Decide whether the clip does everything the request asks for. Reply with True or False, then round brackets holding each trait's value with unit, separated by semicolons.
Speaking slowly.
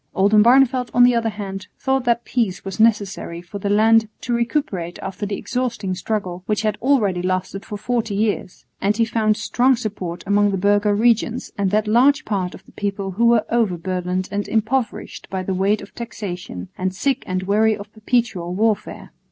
False (185 wpm)